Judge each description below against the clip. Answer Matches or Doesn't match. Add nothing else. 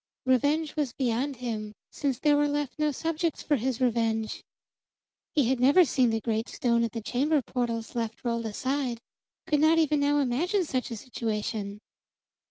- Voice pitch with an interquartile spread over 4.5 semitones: Doesn't match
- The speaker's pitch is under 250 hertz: Doesn't match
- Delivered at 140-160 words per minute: Doesn't match